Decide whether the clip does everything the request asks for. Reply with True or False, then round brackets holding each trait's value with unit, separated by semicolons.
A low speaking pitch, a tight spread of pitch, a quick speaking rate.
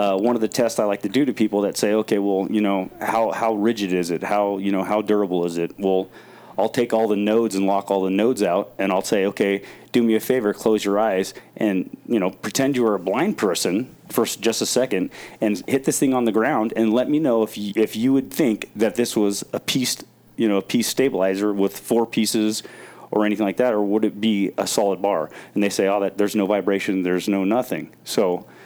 True (105 Hz; 2.1 semitones; 245 wpm)